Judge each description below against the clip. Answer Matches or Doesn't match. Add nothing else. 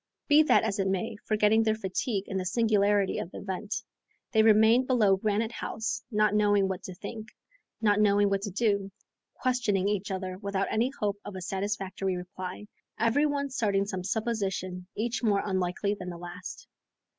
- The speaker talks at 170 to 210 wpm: Matches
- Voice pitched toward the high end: Matches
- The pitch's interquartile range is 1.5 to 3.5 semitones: Matches